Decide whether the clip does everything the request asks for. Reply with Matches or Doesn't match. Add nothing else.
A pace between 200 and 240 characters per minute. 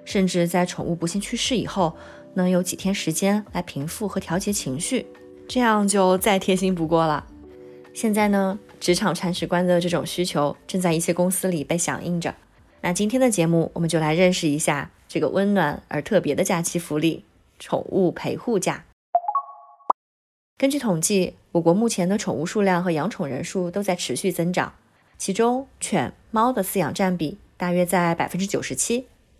Doesn't match